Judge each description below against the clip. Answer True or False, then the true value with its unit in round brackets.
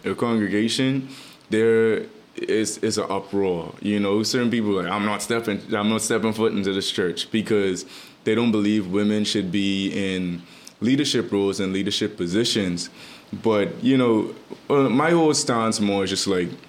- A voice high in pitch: False (105 Hz)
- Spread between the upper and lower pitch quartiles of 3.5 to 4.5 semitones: False (2.6 semitones)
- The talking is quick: False (165 wpm)